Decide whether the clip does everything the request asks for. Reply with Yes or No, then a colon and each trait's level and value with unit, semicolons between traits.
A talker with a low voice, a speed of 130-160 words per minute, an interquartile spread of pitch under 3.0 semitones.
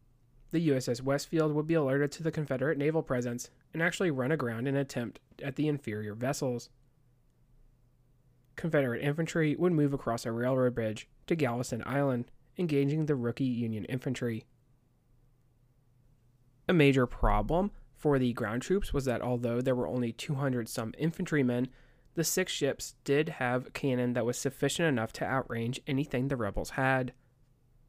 Yes: low, 130 Hz; average, 150 wpm; narrow, 2.6 semitones